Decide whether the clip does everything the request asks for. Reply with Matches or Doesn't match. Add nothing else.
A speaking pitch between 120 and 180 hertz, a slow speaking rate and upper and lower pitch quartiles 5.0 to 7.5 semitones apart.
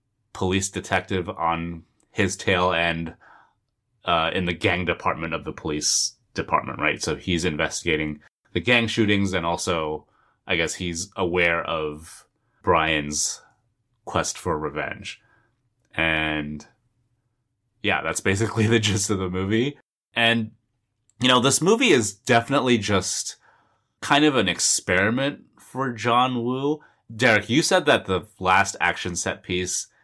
Doesn't match